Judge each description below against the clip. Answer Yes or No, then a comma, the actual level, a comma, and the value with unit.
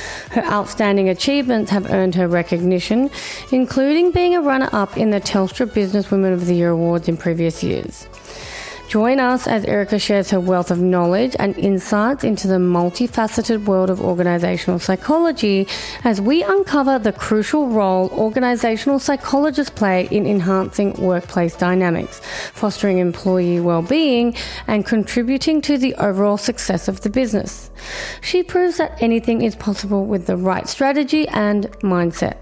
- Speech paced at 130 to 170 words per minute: Yes, average, 145 wpm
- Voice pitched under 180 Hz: No, high, 205 Hz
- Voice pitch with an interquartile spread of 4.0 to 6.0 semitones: Yes, average, 5.3 semitones